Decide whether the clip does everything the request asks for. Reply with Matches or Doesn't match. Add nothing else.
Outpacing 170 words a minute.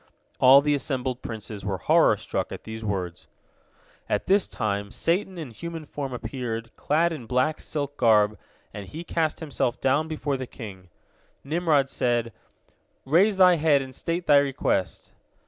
Doesn't match